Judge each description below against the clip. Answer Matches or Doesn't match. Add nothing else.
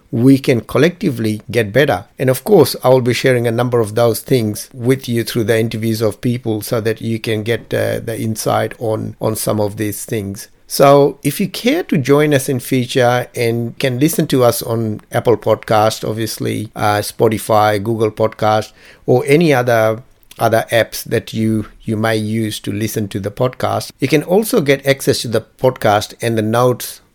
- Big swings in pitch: Doesn't match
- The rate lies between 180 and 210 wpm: Matches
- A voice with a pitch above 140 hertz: Doesn't match